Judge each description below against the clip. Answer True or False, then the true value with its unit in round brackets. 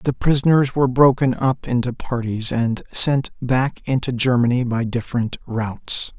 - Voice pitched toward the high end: False (125 Hz)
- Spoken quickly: False (145 wpm)